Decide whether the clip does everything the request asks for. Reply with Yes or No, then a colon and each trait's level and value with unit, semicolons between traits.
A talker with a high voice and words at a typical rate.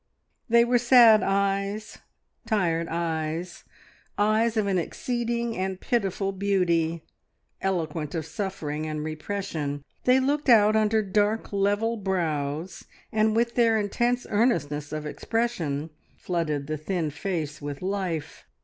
No: high, 195 Hz; slow, 120 wpm